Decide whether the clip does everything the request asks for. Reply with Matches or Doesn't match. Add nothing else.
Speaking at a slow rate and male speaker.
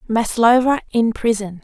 Doesn't match